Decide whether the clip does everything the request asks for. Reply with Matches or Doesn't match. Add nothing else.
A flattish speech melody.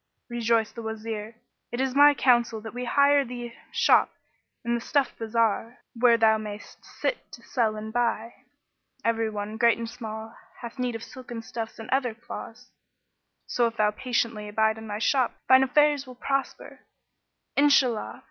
Matches